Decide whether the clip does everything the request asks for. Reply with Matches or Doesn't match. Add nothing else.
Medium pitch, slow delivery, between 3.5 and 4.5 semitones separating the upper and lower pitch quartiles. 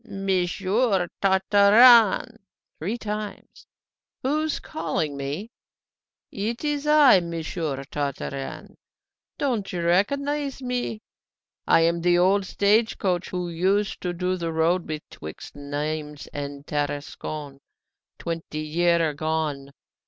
Doesn't match